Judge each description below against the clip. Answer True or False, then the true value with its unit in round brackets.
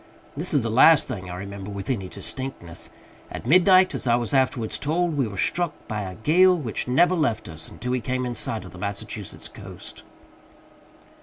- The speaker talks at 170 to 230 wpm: True (190 wpm)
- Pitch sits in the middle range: False (125 Hz)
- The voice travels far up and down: True (7.1 semitones)